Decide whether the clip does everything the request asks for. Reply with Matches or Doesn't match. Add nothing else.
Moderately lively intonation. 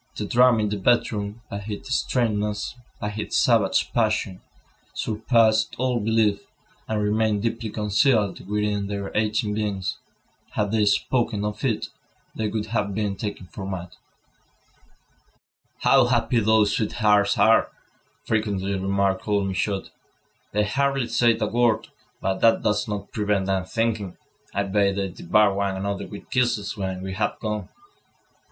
Doesn't match